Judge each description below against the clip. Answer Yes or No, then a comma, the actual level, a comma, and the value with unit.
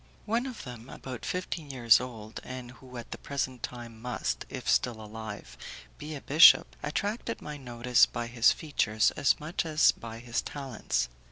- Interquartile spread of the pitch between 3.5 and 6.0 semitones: Yes, average, 4.1 semitones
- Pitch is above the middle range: No, low, 125 Hz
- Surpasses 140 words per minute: Yes, average, 170 wpm